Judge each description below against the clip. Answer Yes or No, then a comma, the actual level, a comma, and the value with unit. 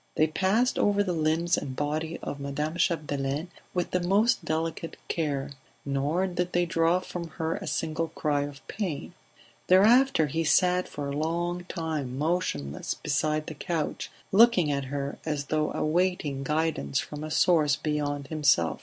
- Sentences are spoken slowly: No, average, 155 wpm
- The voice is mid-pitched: Yes, medium, 155 Hz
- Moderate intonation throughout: Yes, average, 3.4 semitones